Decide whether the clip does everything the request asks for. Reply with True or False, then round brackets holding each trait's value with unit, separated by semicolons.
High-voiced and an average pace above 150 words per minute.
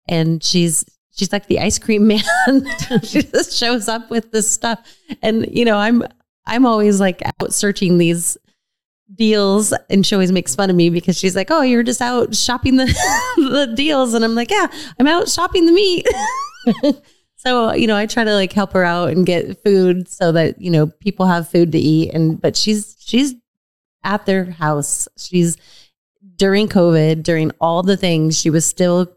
True (205 Hz; 190 wpm)